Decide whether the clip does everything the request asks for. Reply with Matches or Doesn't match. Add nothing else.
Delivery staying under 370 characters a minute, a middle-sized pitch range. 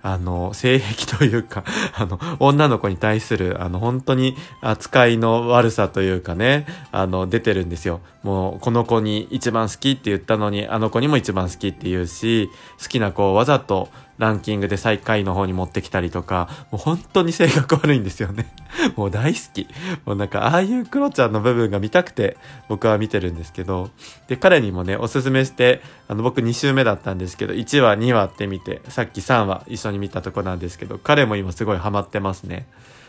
Doesn't match